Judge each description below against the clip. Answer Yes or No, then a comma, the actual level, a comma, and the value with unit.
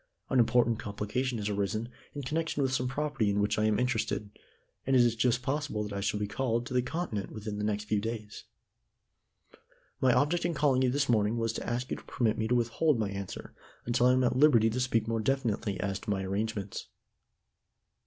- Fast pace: Yes, fast, 215 wpm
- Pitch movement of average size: Yes, average, 3.5 semitones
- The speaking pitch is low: Yes, low, 115 Hz